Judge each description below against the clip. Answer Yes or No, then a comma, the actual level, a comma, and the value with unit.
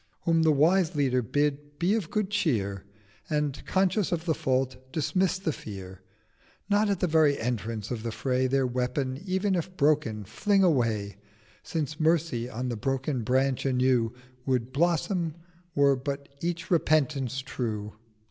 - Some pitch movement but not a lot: Yes, average, 4.9 semitones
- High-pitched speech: No, medium, 140 Hz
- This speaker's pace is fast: No, average, 150 wpm